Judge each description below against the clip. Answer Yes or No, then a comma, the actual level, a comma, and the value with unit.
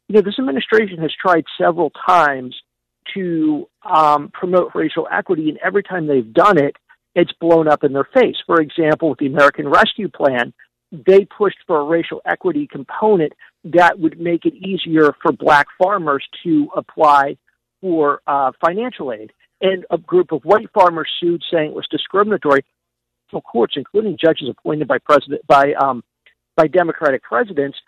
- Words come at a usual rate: Yes, average, 165 wpm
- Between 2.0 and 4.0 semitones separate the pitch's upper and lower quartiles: No, average, 4.6 semitones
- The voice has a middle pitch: Yes, medium, 170 Hz